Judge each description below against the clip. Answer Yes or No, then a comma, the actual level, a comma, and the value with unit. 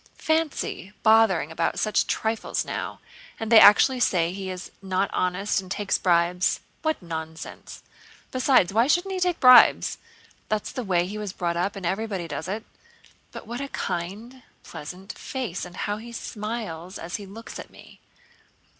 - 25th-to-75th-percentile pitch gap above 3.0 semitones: Yes, average, 4.3 semitones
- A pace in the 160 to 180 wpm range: Yes, average, 165 wpm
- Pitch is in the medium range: No, high, 200 Hz